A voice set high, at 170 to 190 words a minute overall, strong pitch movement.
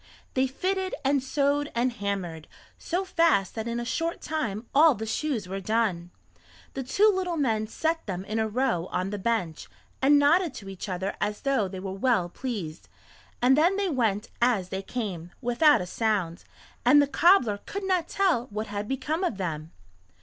Yes: high, 235 Hz; average, 185 wpm; wide, 6.9 semitones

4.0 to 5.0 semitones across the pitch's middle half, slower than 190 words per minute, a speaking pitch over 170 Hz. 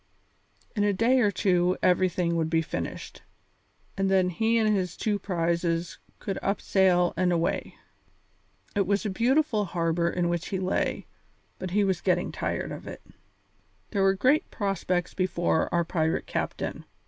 No: average, 2.9 semitones; average, 160 wpm; medium, 185 Hz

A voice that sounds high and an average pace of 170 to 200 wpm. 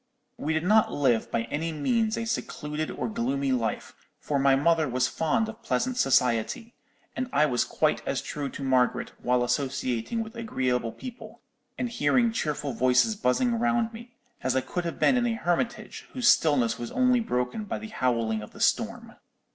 No: medium, 150 Hz; average, 180 wpm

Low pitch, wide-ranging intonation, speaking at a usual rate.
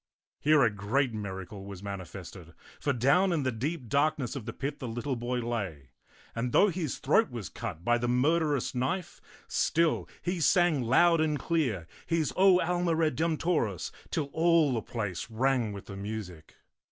Yes: low, 130 Hz; wide, 6.9 semitones; average, 165 wpm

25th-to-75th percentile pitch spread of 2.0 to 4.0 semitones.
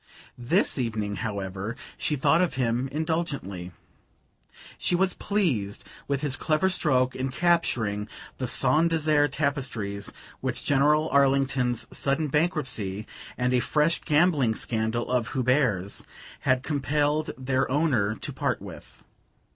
No: average, 4.8 semitones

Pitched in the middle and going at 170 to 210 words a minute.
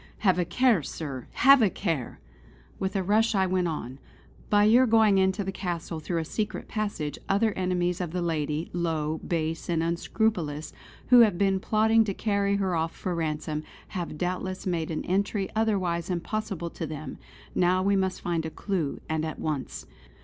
Yes: medium, 180 Hz; average, 180 wpm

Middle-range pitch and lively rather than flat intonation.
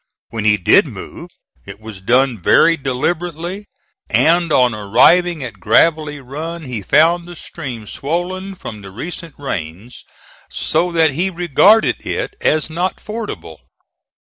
Yes: medium, 150 Hz; wide, 7.5 semitones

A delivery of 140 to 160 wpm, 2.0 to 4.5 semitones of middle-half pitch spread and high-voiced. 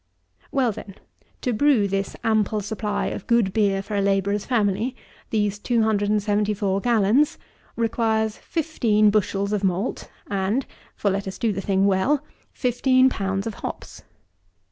Yes: average, 145 wpm; average, 2.7 semitones; high, 210 Hz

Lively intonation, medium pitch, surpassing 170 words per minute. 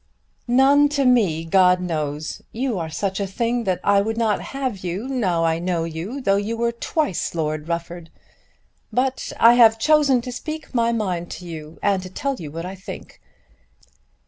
No: wide, 6.3 semitones; high, 200 Hz; average, 180 wpm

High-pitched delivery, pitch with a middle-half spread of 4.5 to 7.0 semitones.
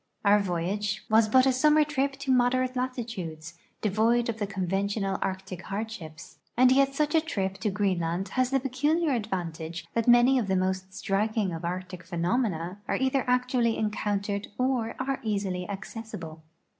Yes: high, 210 Hz; average, 5.2 semitones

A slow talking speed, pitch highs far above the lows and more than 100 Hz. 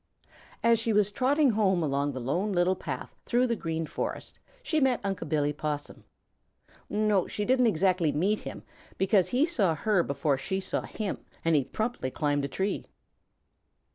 No: average, 170 wpm; wide, 6.3 semitones; high, 190 Hz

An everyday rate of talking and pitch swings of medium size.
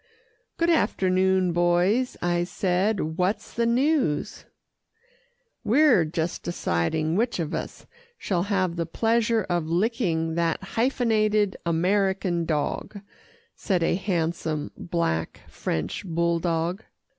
No: slow, 105 wpm; average, 4.2 semitones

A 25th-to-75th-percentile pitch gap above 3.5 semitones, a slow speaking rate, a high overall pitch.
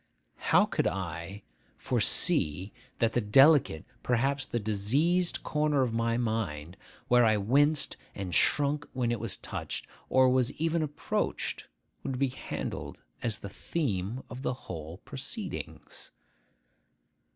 No: wide, 5.5 semitones; slow, 130 wpm; low, 120 Hz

